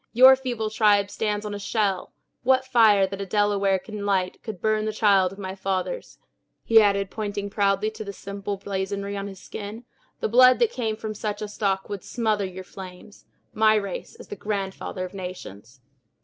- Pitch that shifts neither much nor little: No, narrow, 1.8 semitones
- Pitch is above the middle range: Yes, high, 205 Hz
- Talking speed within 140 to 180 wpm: No, average, 190 wpm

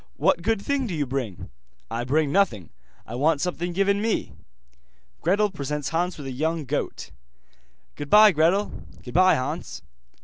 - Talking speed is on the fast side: No, average, 145 wpm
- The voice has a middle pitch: Yes, medium, 165 Hz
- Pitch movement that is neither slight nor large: No, wide, 5.9 semitones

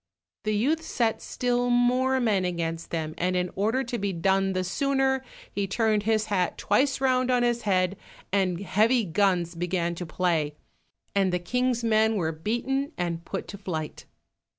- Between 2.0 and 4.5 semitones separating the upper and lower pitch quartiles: No, average, 5.3 semitones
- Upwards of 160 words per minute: Yes, average, 170 wpm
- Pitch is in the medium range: No, high, 200 Hz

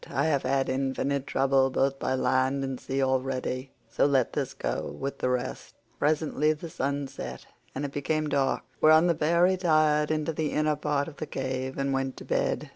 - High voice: No, medium, 140 Hz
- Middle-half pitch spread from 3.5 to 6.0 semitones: No, narrow, 2.4 semitones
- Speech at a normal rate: Yes, average, 195 wpm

